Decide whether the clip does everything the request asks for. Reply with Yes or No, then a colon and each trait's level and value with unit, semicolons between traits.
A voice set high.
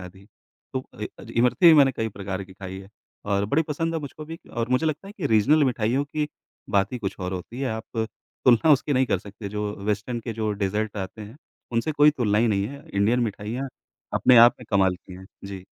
No: low, 115 Hz